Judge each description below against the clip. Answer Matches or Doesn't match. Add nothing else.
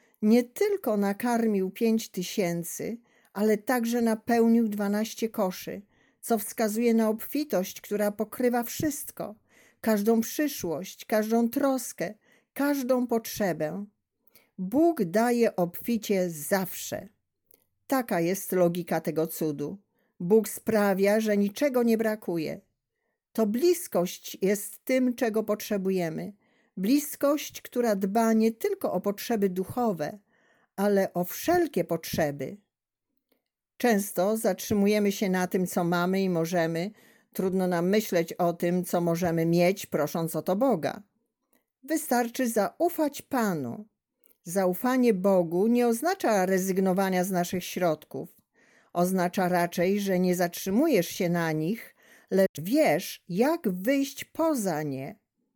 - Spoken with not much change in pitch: Doesn't match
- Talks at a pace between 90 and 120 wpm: Matches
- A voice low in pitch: Doesn't match